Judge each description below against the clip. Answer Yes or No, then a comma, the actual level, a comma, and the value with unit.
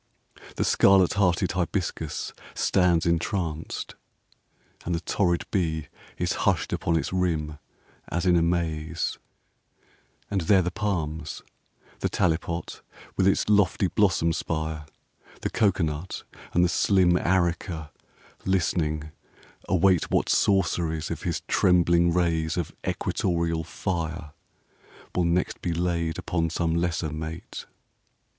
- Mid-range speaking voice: No, very low, 85 Hz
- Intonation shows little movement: Yes, narrow, 2.1 semitones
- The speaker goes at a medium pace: No, slow, 115 wpm